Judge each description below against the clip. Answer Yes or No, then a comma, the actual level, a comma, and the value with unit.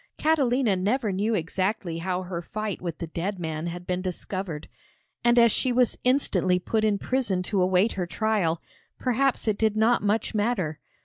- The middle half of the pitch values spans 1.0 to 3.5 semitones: No, average, 4.1 semitones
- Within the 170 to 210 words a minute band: Yes, average, 175 wpm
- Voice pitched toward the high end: Yes, high, 200 Hz